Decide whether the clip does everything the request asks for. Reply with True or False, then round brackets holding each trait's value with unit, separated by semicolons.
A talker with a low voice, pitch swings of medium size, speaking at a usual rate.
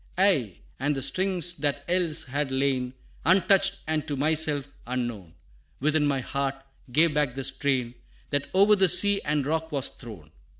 False (145 Hz; 4.0 semitones; 160 wpm)